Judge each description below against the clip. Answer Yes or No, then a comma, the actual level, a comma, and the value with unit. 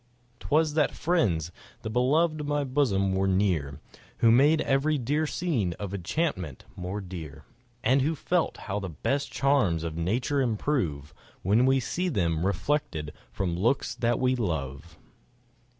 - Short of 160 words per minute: Yes, average, 150 wpm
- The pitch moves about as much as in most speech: No, wide, 8.5 semitones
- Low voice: Yes, low, 115 Hz